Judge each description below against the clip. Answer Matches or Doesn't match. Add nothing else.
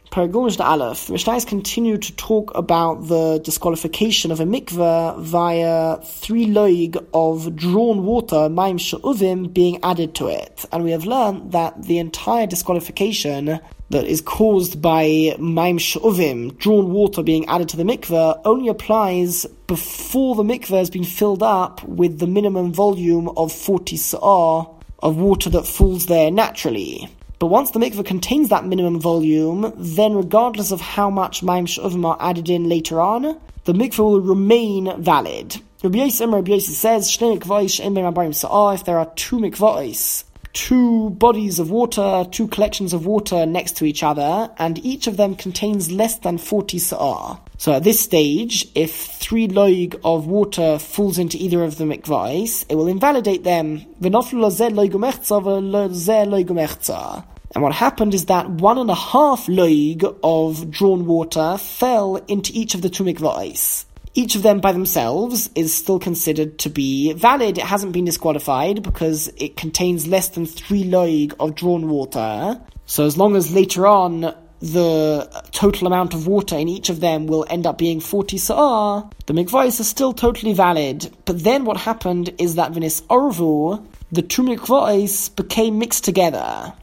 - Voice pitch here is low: Doesn't match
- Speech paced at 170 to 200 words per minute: Doesn't match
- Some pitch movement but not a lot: Matches